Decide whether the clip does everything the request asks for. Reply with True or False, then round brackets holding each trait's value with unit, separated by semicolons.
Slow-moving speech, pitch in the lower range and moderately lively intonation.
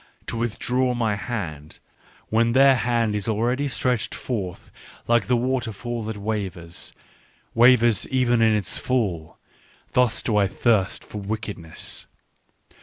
True (130 wpm; 115 Hz; 3.0 semitones)